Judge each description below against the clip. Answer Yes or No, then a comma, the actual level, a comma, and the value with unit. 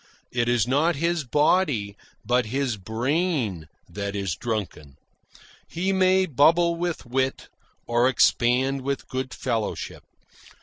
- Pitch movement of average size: No, wide, 6.1 semitones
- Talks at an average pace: No, slow, 120 wpm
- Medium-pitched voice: No, low, 130 Hz